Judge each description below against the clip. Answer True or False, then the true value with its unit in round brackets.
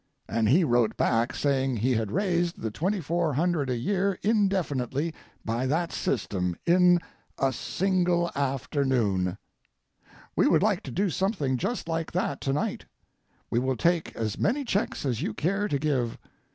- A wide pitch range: True (6.3 semitones)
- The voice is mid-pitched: True (150 Hz)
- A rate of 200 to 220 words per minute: False (150 wpm)